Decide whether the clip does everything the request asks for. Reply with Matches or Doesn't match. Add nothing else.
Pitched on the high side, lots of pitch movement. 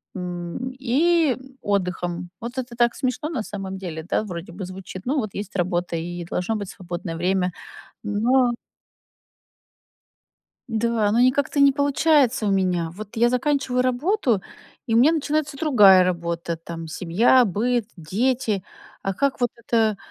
Matches